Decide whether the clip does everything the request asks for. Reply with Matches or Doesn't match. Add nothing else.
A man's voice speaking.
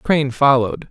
Matches